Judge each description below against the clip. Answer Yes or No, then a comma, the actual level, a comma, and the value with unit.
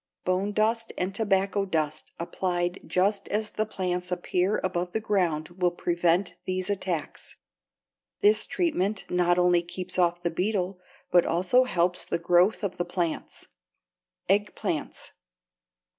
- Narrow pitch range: Yes, narrow, 2.3 semitones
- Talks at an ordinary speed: No, slow, 130 wpm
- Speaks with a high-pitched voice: No, medium, 180 Hz